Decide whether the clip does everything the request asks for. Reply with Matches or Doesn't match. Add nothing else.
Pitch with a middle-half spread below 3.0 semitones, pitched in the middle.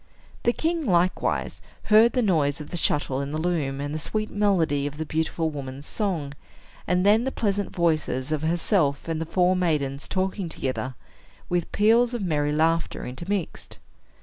Doesn't match